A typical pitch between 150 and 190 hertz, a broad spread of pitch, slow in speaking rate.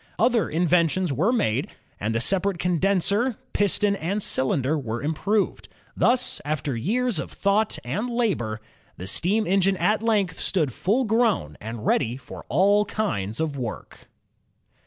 No: medium, 185 Hz; wide, 7.4 semitones; average, 145 wpm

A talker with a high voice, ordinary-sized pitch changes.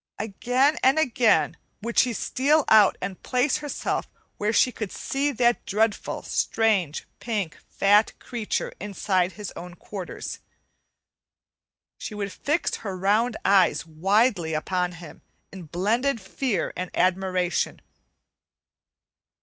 Yes: high, 210 Hz; average, 4.7 semitones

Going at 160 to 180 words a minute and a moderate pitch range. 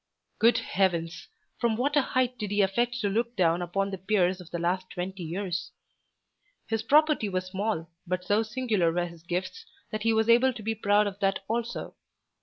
No: average, 195 wpm; average, 3.9 semitones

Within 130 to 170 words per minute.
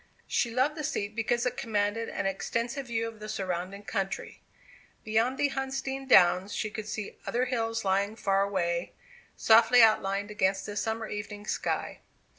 Yes: average, 160 wpm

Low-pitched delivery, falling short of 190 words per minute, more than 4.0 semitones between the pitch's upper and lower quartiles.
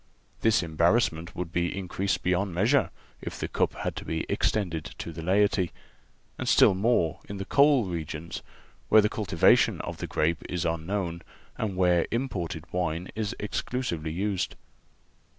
No: very low, 90 Hz; average, 150 wpm; average, 3.7 semitones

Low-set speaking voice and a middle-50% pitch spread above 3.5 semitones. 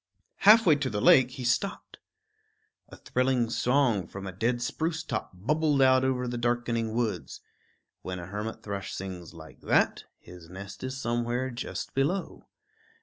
Yes: low, 120 Hz; average, 4.8 semitones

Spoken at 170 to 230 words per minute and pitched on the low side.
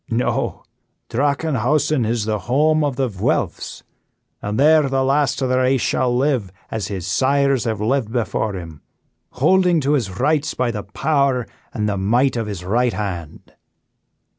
No: average, 160 wpm; low, 125 Hz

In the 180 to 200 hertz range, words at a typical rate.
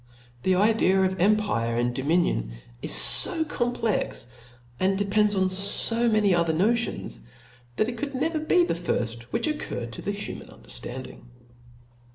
Yes: high, 190 Hz; average, 145 wpm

